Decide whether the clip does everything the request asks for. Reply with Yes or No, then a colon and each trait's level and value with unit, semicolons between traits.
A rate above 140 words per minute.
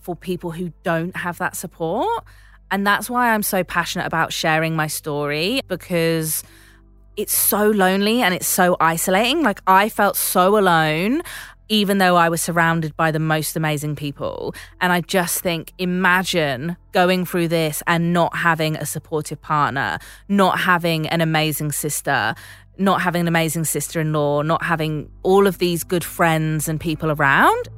Yes: average, 165 wpm